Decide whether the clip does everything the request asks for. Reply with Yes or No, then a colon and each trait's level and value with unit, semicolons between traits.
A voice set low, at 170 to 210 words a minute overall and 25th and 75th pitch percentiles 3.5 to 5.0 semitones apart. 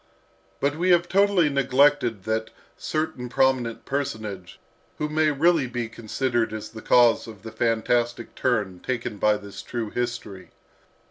No: low, 120 Hz; average, 140 wpm; average, 4.1 semitones